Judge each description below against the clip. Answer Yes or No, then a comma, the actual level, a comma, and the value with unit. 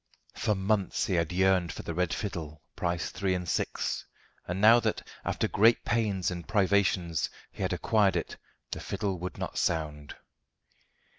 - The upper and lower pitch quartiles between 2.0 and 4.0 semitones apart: Yes, average, 2.9 semitones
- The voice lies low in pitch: Yes, very low, 95 Hz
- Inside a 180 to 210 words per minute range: No, average, 160 wpm